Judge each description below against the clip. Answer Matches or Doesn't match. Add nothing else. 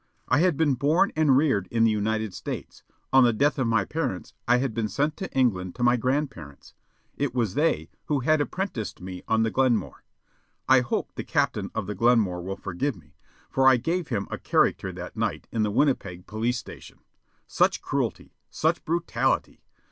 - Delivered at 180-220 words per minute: Matches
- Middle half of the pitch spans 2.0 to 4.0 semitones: Doesn't match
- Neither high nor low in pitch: Doesn't match